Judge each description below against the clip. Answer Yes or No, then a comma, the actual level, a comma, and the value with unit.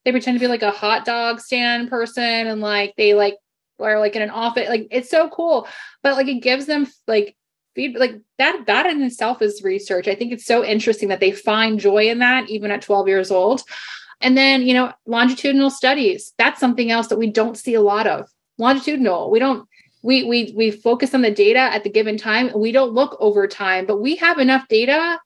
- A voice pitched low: No, high, 235 Hz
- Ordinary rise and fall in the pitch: Yes, average, 3.5 semitones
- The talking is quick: Yes, fast, 220 wpm